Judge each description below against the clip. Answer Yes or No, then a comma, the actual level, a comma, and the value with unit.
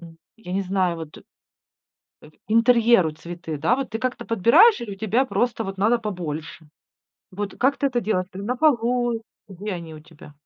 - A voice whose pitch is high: Yes, high, 205 Hz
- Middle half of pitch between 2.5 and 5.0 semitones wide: No, wide, 5.4 semitones